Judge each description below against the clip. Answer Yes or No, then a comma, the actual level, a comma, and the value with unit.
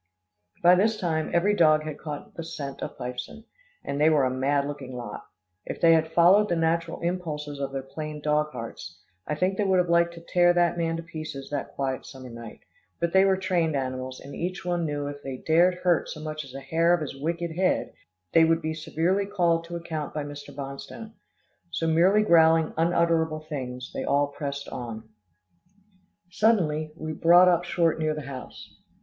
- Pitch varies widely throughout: No, average, 3.2 semitones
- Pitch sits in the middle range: Yes, medium, 160 Hz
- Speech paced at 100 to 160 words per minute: No, average, 195 wpm